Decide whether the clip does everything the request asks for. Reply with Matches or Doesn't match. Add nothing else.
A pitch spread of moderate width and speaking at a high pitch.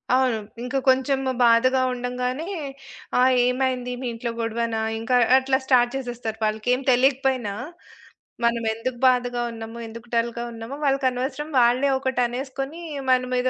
Doesn't match